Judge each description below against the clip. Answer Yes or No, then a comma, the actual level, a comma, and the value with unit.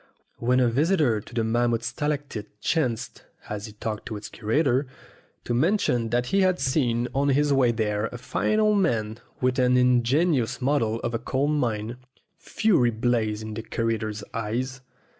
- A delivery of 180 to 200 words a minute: No, average, 165 wpm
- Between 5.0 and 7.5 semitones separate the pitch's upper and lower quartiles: No, average, 3.8 semitones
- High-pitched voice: No, low, 120 Hz